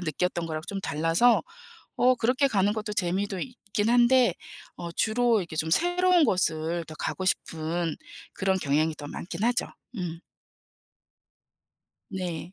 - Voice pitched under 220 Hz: Yes, high, 190 Hz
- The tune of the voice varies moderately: No, wide, 6.2 semitones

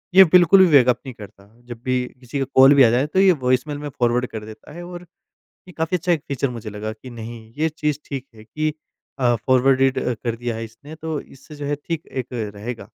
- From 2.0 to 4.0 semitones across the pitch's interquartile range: No, average, 4.4 semitones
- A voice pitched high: No, low, 130 Hz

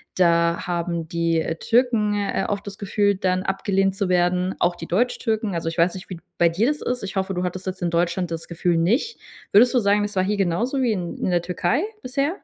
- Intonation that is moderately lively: Yes, average, 3.3 semitones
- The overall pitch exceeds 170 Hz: Yes, high, 190 Hz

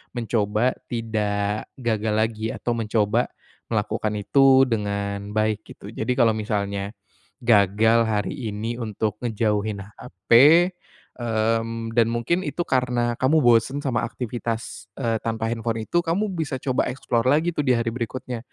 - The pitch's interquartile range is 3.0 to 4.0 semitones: No, narrow, 2.6 semitones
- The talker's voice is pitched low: Yes, low, 115 Hz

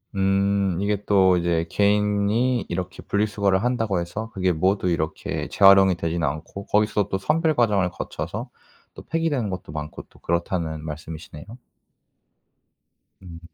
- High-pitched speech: No, very low, 95 Hz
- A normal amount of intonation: Yes, average, 3.3 semitones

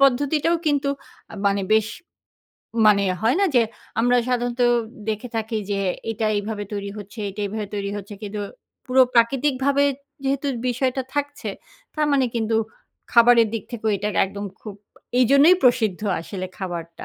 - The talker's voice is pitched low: No, high, 230 Hz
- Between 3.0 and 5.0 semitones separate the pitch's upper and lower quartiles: Yes, average, 4.4 semitones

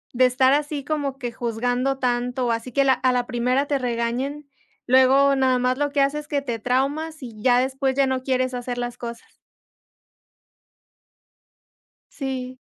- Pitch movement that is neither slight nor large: No, narrow, 2.0 semitones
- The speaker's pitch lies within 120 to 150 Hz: No, very high, 255 Hz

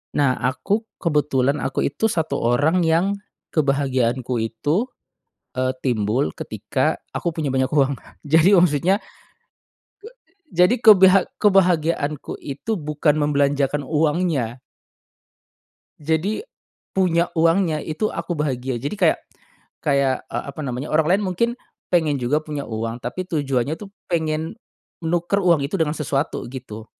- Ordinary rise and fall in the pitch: Yes, average, 4.2 semitones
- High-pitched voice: No, medium, 150 Hz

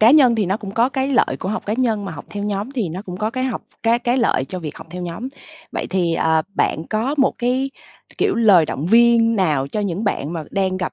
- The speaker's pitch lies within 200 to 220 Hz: Yes, high, 210 Hz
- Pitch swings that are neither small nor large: Yes, average, 4.9 semitones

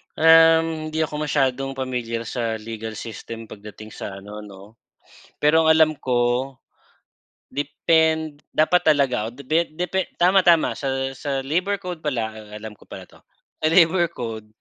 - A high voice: No, low, 135 Hz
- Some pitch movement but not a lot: No, wide, 5.8 semitones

